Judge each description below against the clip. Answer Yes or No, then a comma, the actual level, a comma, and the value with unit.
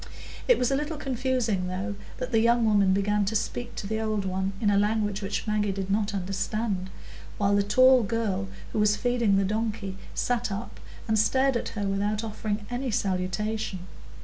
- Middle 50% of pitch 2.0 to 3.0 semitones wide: Yes, average, 2.7 semitones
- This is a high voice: Yes, high, 210 Hz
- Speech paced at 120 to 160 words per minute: No, average, 185 wpm